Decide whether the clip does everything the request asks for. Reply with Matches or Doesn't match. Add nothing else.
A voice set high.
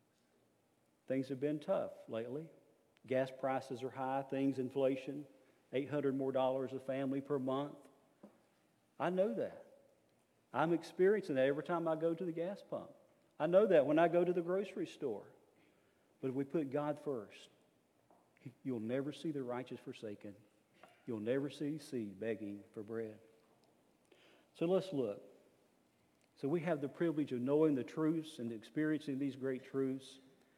Doesn't match